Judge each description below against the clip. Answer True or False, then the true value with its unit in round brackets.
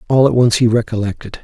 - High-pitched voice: False (115 Hz)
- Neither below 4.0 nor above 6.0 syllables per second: False (6.5 syllables/s)